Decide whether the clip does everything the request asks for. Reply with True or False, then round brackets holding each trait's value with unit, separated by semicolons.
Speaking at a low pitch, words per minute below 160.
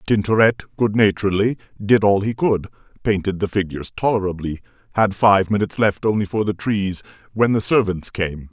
True (100 Hz; 150 wpm)